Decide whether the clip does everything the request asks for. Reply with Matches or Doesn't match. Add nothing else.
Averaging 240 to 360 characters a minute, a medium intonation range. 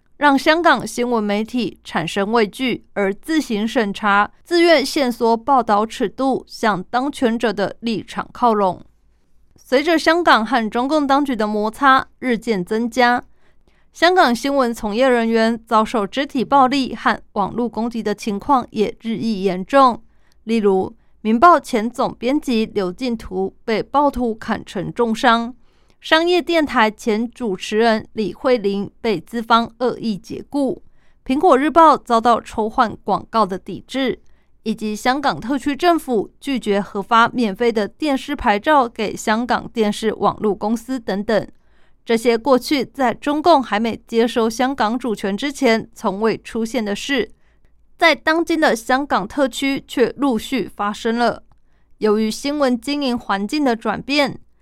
Doesn't match